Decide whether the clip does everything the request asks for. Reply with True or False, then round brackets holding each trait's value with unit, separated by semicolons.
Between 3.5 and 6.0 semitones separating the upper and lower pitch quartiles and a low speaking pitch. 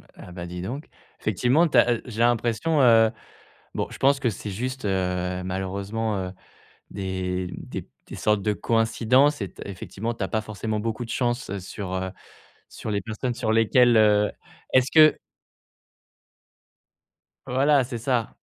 True (4.0 semitones; 110 Hz)